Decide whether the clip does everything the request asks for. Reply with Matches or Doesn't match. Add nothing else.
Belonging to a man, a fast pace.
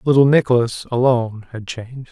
Doesn't match